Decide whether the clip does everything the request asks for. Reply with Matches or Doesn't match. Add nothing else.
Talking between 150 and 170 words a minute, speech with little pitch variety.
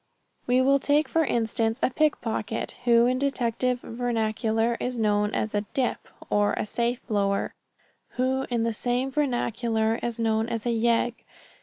Matches